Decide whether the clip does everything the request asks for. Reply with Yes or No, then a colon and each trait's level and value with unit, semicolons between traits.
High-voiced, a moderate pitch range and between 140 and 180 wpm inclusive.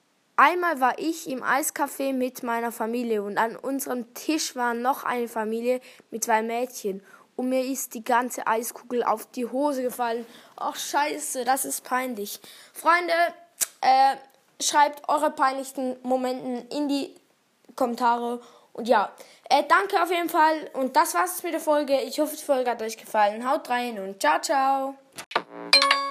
Yes: very high, 260 Hz; average, 3.6 semitones; average, 155 wpm